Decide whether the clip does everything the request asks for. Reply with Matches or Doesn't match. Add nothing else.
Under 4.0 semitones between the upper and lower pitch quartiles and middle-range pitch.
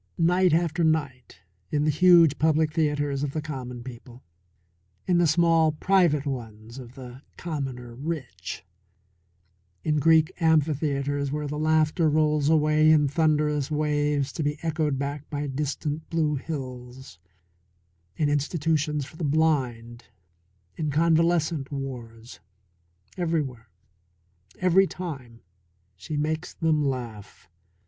Matches